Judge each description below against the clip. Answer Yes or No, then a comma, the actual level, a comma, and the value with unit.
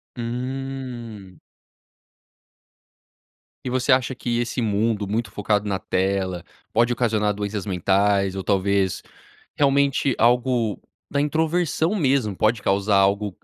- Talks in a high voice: No, low, 110 Hz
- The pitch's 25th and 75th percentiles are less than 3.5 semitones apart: No, average, 4.3 semitones